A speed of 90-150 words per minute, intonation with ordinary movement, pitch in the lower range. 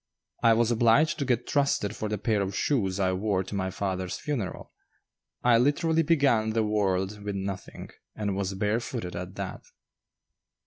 No: average, 165 wpm; average, 3.6 semitones; low, 105 Hz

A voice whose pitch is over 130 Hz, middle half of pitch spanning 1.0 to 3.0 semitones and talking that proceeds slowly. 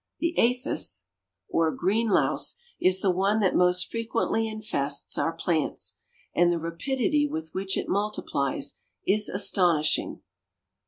No: medium, 185 Hz; average, 4.8 semitones; slow, 125 wpm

